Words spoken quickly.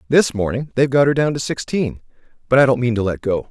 Yes: fast, 255 wpm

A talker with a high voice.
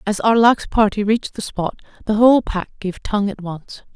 Yes: high, 210 Hz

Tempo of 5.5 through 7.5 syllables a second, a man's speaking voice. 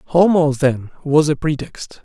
No: 4.4 syllables/s; male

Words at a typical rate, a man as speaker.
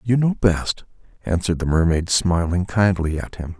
Yes: average, 165 wpm; male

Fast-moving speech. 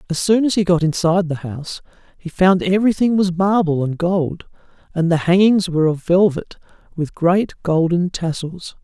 No: average, 170 wpm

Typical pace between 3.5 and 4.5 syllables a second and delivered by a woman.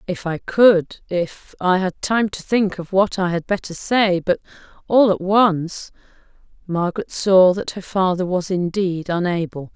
Yes: 4.3 syllables/s; female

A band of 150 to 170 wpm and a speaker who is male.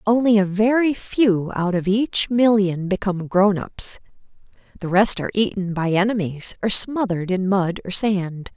No: average, 155 wpm; female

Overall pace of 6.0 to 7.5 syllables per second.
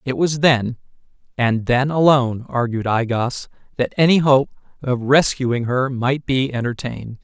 No: 4.4 syllables/s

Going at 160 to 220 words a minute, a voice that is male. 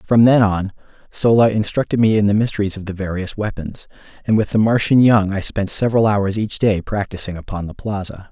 Yes: average, 200 wpm; male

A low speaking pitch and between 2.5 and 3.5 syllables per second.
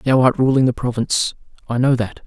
No: low, 125 Hz; 5.8 syllables/s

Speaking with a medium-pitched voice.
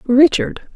No: very high, 270 Hz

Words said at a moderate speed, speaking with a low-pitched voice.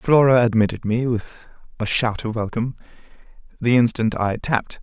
Yes: average, 150 wpm; low, 115 Hz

